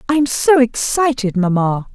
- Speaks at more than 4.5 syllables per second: No, 4.0 syllables/s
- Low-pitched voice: No, high, 240 Hz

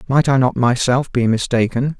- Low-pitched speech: Yes, low, 125 Hz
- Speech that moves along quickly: No, average, 180 wpm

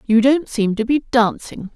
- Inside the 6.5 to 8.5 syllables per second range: No, 4.3 syllables/s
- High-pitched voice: Yes, high, 235 Hz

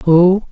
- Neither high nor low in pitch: Yes, medium, 180 Hz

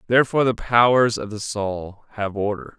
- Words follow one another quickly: No, average, 170 wpm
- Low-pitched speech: Yes, low, 110 Hz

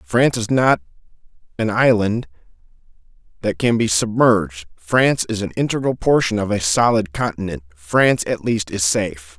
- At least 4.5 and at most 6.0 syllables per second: Yes, 5.1 syllables/s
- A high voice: No, low, 105 Hz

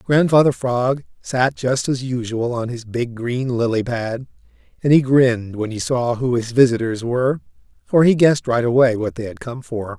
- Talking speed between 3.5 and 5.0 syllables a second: Yes, 4.7 syllables/s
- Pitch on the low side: Yes, low, 120 Hz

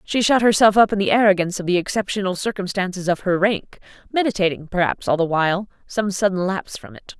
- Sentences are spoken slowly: No, average, 200 wpm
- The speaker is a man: No, female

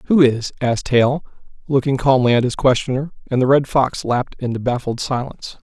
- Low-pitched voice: Yes, low, 130 Hz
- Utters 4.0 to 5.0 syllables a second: No, 5.7 syllables/s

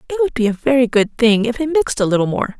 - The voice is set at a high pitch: Yes, high, 240 Hz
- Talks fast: Yes, fast, 300 wpm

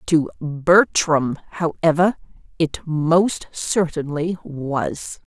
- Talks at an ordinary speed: No, slow, 80 wpm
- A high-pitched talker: No, medium, 165 Hz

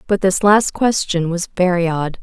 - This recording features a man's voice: No, female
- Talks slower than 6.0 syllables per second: Yes, 4.5 syllables/s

